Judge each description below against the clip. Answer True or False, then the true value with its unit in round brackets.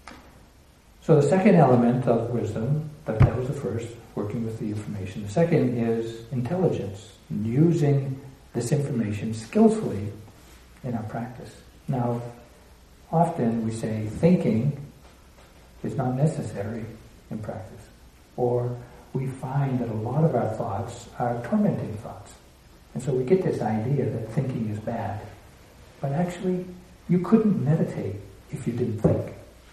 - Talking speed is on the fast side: False (135 wpm)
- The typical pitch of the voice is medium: False (120 Hz)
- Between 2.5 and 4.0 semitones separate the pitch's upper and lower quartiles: False (4.8 semitones)